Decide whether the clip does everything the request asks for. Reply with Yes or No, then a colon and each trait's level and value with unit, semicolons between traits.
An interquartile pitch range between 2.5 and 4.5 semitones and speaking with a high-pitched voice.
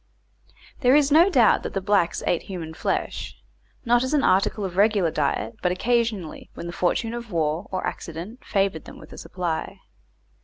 No: wide, 5.5 semitones; high, 195 Hz